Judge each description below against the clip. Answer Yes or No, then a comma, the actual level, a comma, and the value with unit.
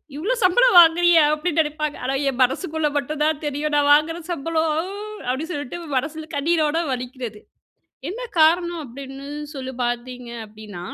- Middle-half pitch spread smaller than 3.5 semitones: No, average, 3.8 semitones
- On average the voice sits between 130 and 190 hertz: No, very high, 300 Hz